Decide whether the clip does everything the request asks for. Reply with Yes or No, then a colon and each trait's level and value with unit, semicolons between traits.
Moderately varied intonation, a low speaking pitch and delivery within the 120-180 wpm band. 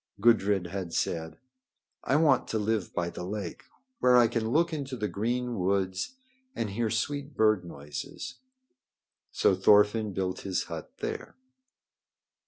Yes: average, 4.4 semitones; low, 105 Hz; average, 140 wpm